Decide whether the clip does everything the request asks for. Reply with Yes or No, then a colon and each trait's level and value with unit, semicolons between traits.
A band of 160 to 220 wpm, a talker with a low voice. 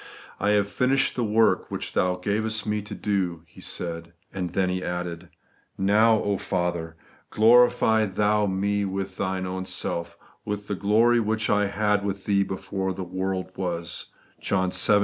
Yes: average, 170 wpm; low, 100 Hz